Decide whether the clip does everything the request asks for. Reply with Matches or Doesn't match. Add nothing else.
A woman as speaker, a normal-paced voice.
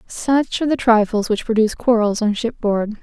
Matches